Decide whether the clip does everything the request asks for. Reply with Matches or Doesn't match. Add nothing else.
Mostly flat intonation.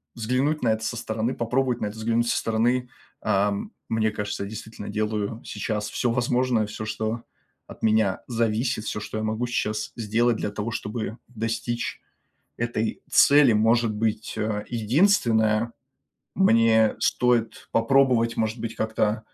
Matches